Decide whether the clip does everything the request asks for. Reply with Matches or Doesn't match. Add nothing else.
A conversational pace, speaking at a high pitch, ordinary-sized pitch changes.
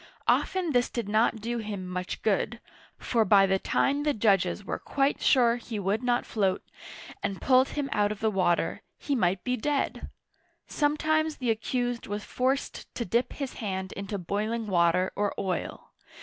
Matches